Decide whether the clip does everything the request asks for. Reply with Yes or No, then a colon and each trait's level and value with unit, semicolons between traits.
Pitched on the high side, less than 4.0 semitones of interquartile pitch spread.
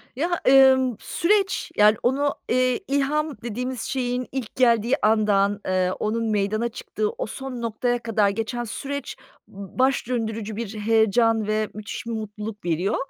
Yes: high, 230 Hz; average, 3.6 semitones